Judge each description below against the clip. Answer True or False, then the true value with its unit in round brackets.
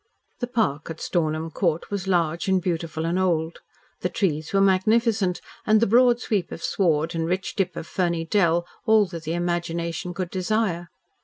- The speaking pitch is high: False (175 Hz)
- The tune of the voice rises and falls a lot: False (3.0 semitones)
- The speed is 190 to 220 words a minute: False (175 wpm)